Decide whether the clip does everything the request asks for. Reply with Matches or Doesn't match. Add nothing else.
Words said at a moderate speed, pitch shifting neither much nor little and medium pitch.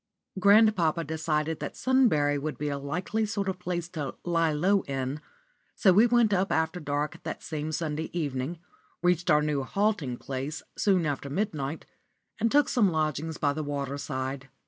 Matches